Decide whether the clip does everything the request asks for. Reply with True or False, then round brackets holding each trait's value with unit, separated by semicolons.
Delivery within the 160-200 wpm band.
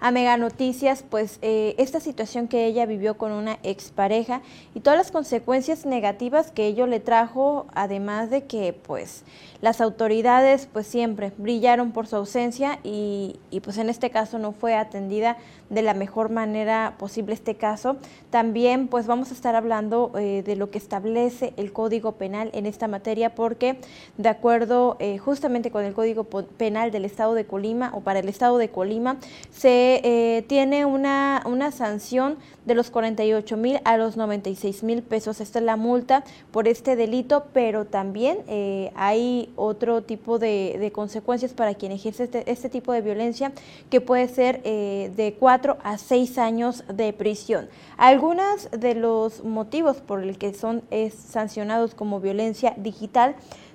True (165 wpm)